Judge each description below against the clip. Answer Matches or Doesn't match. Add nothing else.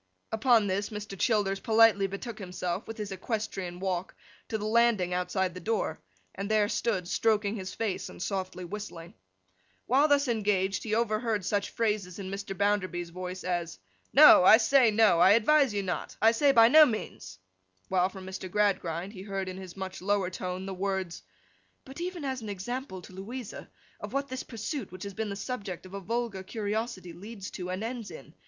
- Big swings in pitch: Doesn't match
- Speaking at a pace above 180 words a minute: Matches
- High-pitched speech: Matches